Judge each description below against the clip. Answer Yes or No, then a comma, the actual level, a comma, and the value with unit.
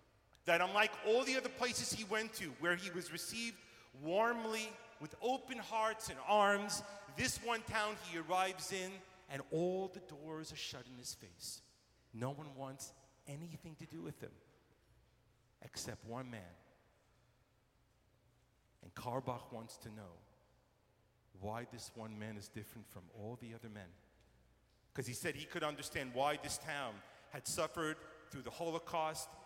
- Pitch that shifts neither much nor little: No, wide, 7.7 semitones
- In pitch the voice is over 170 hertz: No, medium, 145 Hz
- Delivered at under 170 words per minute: Yes, average, 155 wpm